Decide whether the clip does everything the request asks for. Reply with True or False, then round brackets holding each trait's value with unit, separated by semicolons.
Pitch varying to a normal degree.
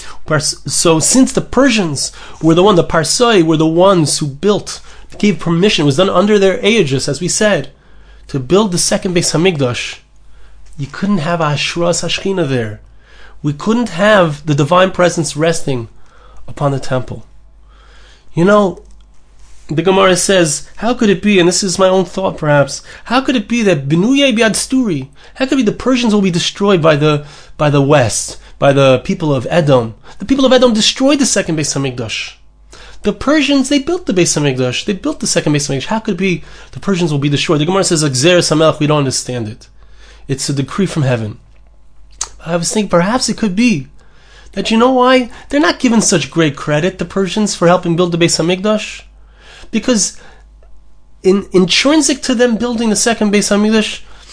False (5.9 semitones)